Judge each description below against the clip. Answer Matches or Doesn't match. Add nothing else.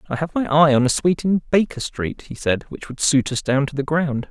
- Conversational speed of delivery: Doesn't match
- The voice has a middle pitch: Matches